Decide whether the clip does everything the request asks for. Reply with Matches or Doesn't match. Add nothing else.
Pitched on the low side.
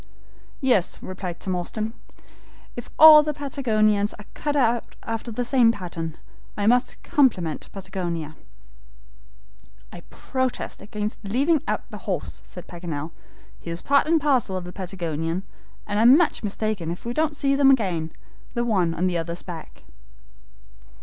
Doesn't match